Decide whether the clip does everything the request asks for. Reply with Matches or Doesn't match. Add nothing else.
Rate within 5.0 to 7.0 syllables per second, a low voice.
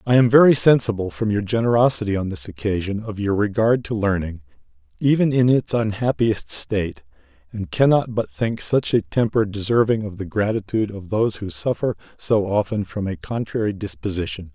Matches